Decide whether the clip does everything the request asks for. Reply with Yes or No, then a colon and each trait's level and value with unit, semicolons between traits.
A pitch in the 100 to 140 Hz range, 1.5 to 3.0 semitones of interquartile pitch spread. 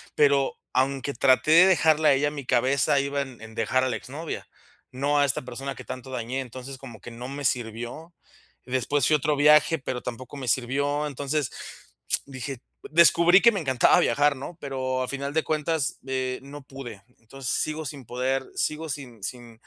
Yes: low, 135 Hz; narrow, 2.5 semitones